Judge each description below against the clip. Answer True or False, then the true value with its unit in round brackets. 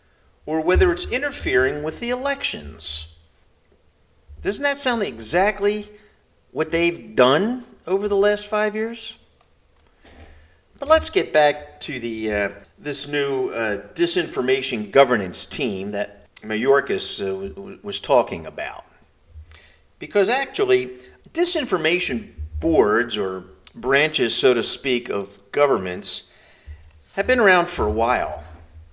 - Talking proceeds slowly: True (120 wpm)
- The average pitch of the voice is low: False (145 Hz)